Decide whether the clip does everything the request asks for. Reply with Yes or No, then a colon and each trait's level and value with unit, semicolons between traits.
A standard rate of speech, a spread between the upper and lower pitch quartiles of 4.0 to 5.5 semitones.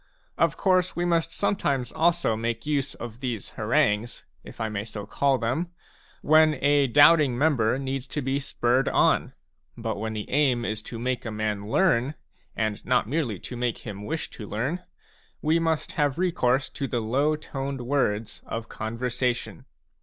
Yes: average, 170 wpm; average, 4.7 semitones